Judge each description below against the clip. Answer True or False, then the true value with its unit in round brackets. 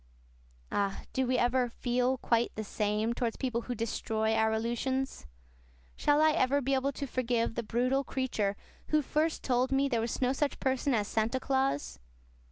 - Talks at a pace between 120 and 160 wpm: False (175 wpm)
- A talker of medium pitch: False (250 Hz)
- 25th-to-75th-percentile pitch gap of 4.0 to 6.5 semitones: False (2.9 semitones)